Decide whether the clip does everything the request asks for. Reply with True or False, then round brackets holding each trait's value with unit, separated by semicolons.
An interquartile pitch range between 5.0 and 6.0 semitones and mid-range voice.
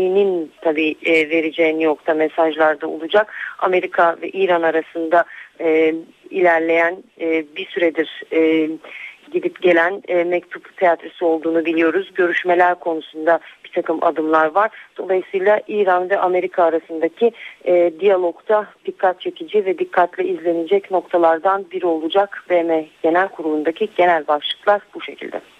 False (2.7 semitones; 175 Hz)